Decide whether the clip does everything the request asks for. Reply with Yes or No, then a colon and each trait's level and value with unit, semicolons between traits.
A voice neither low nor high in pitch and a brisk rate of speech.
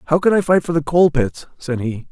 Yes: medium, 155 Hz; fast, 285 wpm